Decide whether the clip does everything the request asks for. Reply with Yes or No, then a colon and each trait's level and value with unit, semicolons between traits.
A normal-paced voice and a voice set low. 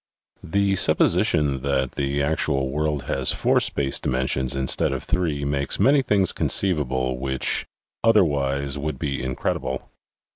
No: slow, 130 wpm; very low, 70 Hz